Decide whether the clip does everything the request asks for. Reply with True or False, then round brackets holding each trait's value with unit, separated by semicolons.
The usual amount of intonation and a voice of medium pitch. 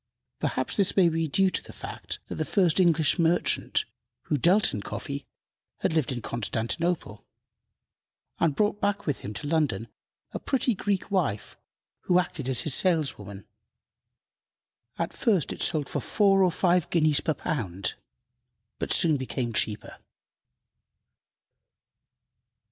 False (5.8 semitones; 160 Hz)